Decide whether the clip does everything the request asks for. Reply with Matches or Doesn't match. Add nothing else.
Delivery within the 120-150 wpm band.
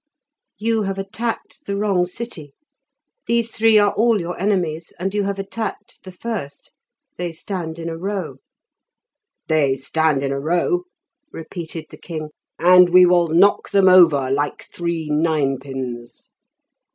Matches